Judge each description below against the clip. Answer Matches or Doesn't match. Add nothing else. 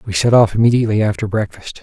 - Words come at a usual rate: Matches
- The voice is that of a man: Matches